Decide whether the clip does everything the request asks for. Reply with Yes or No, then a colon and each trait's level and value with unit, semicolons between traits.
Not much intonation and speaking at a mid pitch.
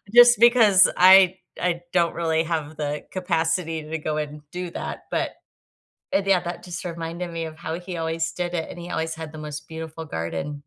Yes: narrow, 2.1 semitones; medium, 165 Hz